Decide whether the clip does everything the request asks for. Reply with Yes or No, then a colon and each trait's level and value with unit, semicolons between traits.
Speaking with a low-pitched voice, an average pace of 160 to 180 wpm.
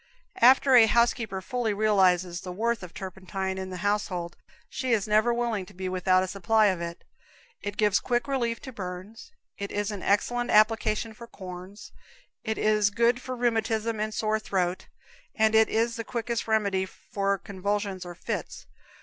No: high, 210 Hz; average, 170 wpm